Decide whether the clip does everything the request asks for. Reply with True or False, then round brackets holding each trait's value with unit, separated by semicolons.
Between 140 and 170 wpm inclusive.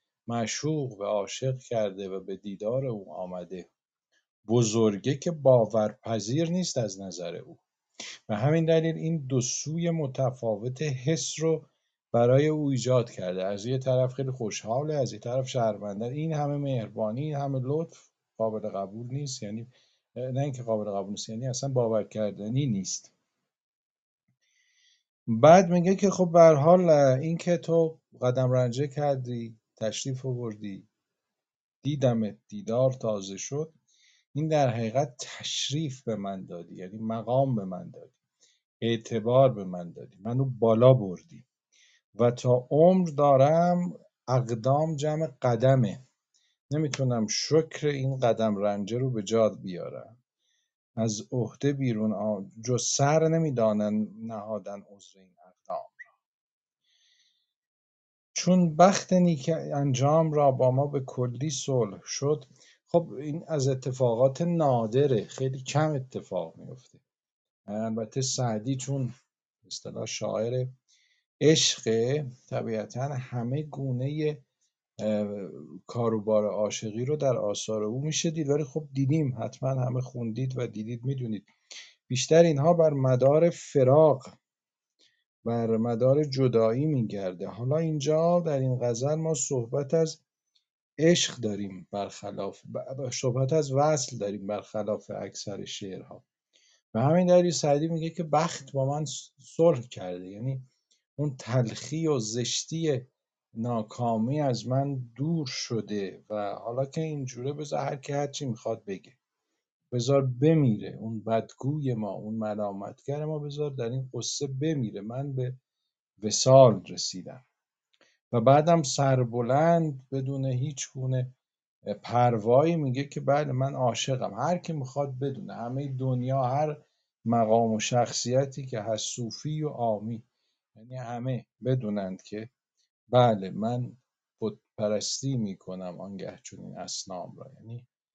False (125 wpm)